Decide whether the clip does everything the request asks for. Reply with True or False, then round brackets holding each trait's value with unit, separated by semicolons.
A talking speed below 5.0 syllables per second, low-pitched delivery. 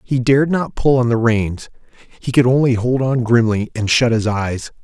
True (4.7 syllables/s; 120 Hz)